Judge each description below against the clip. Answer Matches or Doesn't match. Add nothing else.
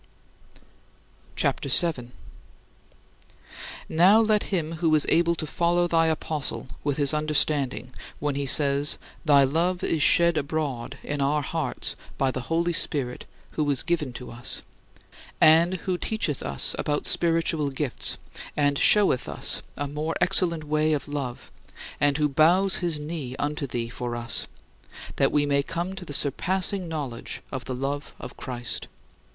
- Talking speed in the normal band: Matches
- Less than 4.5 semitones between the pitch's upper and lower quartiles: Matches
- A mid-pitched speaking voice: Matches